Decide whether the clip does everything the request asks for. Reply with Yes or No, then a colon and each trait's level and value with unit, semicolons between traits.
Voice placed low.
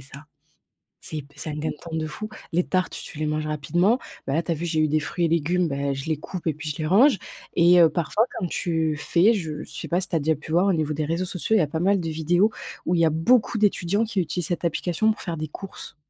No: medium, 165 Hz